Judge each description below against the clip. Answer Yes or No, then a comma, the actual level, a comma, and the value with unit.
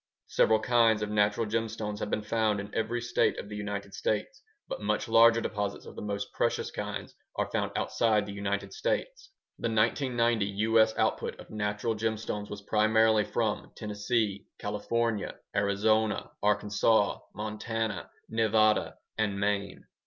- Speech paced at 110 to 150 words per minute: Yes, average, 145 wpm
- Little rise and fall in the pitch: Yes, narrow, 1.5 semitones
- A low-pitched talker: Yes, low, 110 Hz